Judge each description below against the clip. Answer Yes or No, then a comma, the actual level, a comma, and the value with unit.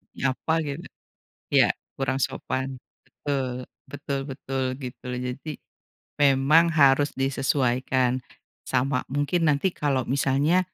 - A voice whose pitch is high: No, low, 135 Hz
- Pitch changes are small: Yes, narrow, 1.8 semitones